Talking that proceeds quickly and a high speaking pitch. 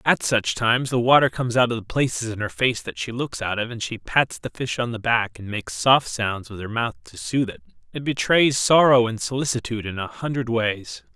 No: fast, 240 wpm; low, 115 Hz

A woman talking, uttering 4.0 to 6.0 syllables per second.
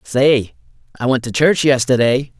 No: male; 4.4 syllables/s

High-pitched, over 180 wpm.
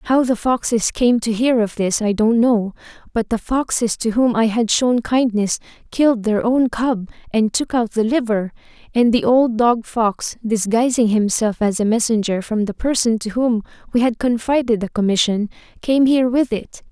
Yes: high, 230 Hz; average, 190 wpm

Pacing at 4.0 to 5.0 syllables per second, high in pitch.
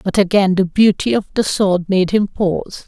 Yes: 4.8 syllables/s; high, 195 Hz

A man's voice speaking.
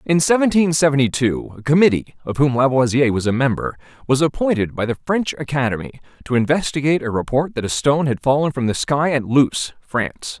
Yes: male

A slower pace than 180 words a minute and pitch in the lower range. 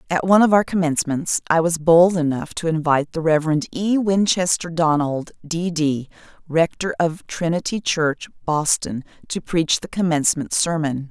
No: average, 150 wpm; medium, 165 Hz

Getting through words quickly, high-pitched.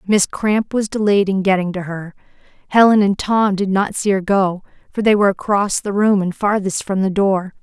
Yes: fast, 210 wpm; high, 195 Hz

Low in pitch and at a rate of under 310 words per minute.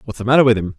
No: low, 115 Hz; fast, 385 wpm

